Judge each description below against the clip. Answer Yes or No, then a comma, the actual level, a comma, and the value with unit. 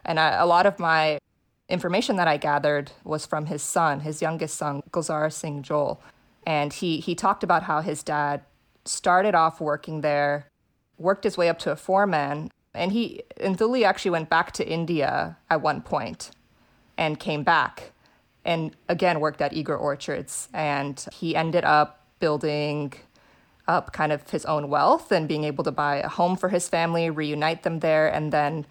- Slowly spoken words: No, average, 180 wpm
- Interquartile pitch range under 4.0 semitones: Yes, narrow, 2.4 semitones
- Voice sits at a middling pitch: Yes, medium, 155 Hz